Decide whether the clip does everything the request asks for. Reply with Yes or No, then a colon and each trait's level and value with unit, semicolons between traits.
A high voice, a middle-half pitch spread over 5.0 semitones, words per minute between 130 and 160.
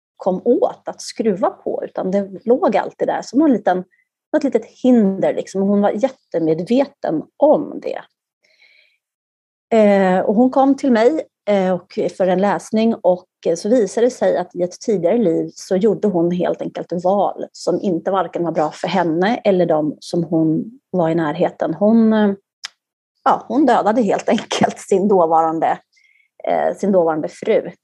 Yes: high, 195 Hz; wide, 5.4 semitones; average, 150 wpm